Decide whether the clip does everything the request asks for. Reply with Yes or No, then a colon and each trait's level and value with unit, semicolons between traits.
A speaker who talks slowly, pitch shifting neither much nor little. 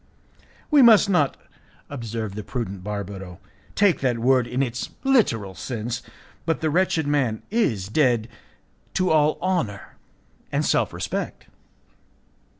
No: slow, 125 wpm; wide, 7.1 semitones